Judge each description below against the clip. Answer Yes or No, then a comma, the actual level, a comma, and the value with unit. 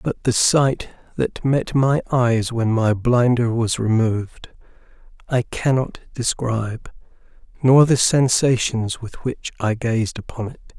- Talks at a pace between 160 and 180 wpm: No, slow, 135 wpm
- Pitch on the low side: Yes, low, 120 Hz